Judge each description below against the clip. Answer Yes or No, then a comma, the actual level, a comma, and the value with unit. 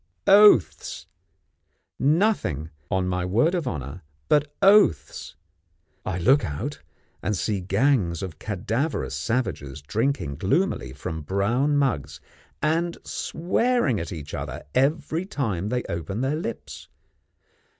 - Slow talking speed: Yes, slow, 115 wpm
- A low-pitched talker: Yes, low, 110 Hz